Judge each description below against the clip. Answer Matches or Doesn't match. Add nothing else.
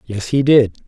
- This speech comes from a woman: Doesn't match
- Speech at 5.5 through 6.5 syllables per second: Doesn't match